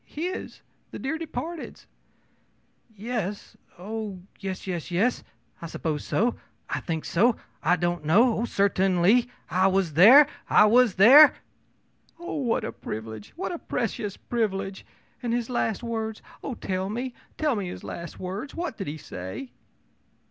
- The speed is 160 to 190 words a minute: No, average, 150 wpm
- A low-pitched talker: No, high, 210 Hz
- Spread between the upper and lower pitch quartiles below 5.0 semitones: No, average, 5.3 semitones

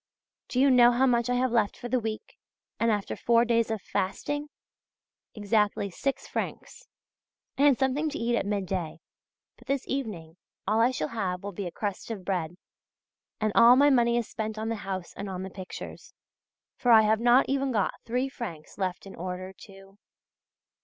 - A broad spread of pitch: No, average, 4.1 semitones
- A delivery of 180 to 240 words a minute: Yes, average, 185 wpm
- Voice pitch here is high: Yes, high, 220 Hz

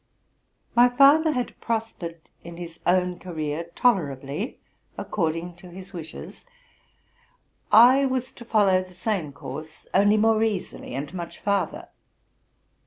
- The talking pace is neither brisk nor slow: No, slow, 120 wpm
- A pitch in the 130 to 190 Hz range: Yes, medium, 185 Hz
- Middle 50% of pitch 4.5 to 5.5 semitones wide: Yes, average, 5.1 semitones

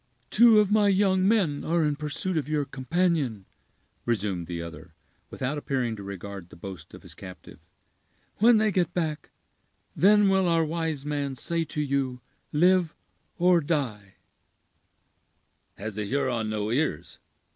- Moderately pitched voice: Yes, medium, 145 Hz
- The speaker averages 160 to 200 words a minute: No, average, 145 wpm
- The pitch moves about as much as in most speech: No, wide, 8.6 semitones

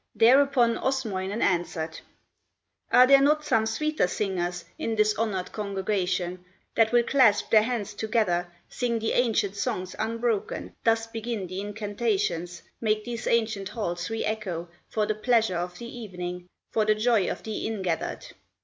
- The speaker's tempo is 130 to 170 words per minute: Yes, average, 150 wpm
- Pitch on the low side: No, high, 215 Hz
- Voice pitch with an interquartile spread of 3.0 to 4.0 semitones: Yes, average, 3.7 semitones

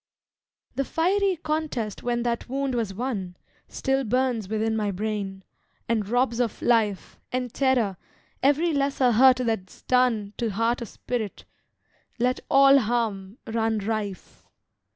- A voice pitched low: No, high, 235 Hz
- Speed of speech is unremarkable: No, slow, 130 wpm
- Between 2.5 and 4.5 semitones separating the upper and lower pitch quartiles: Yes, average, 3.5 semitones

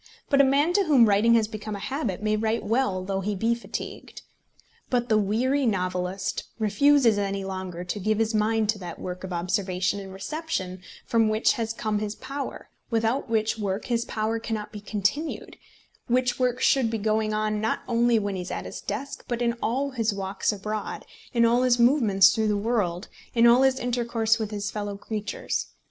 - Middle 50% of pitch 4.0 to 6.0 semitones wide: No, average, 3.0 semitones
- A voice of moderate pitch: No, high, 220 Hz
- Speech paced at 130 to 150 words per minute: No, average, 195 wpm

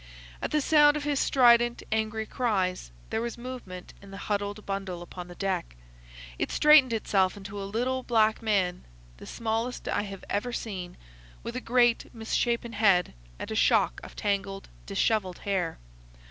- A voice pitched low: No, high, 210 Hz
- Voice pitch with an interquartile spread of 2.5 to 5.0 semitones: Yes, average, 4.0 semitones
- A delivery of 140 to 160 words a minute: Yes, average, 155 wpm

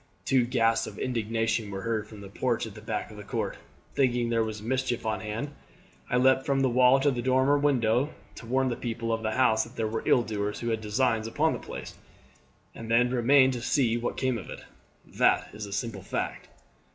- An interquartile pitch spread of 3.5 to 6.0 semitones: No, average, 2.7 semitones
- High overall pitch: No, low, 115 Hz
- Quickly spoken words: Yes, fast, 225 wpm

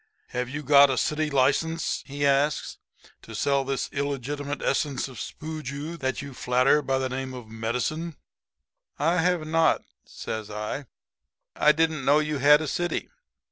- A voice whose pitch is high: No, medium, 140 Hz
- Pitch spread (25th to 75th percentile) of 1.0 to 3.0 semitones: Yes, narrow, 2.6 semitones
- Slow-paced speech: No, average, 155 wpm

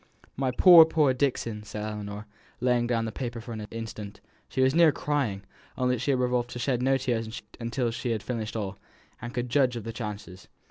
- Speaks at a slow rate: No, fast, 205 wpm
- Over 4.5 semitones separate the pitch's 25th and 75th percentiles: No, average, 3.1 semitones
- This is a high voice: No, low, 120 Hz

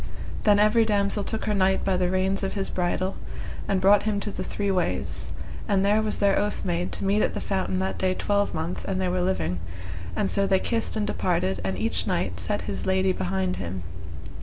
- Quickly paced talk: Yes, fast, 210 wpm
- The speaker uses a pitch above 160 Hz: Yes, high, 190 Hz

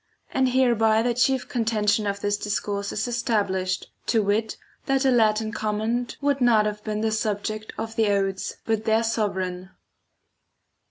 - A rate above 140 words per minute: Yes, average, 155 wpm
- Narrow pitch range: Yes, narrow, 2.3 semitones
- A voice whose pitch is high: Yes, high, 220 Hz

